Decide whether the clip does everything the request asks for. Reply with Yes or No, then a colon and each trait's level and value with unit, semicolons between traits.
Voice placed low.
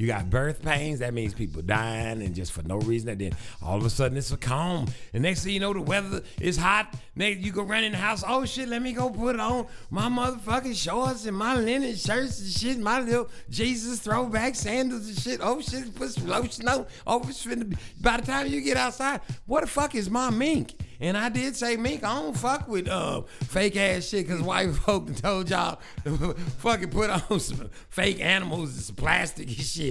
No: high, 195 Hz